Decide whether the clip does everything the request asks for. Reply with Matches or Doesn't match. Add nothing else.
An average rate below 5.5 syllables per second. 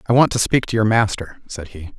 Doesn't match